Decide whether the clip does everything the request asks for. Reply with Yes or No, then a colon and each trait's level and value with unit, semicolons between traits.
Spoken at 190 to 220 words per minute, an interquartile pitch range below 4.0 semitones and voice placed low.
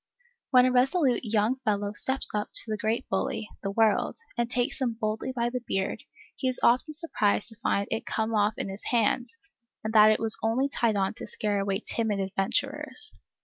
No: average, 195 wpm; average, 3.3 semitones; high, 225 Hz